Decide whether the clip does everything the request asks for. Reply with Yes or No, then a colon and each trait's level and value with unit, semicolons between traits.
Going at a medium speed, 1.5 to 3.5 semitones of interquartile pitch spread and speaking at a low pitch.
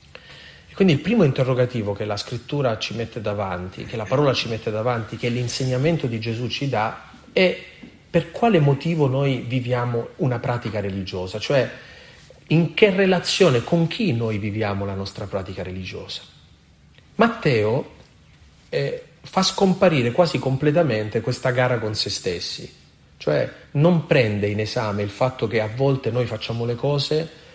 No: average, 150 wpm; wide, 5.5 semitones; low, 120 Hz